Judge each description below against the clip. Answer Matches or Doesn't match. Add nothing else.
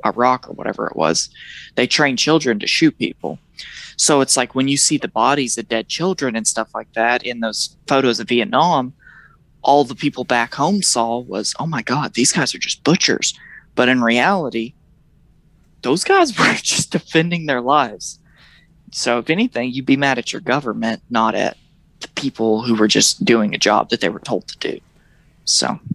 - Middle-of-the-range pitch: Doesn't match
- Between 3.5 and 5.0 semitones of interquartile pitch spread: Matches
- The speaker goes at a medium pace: Matches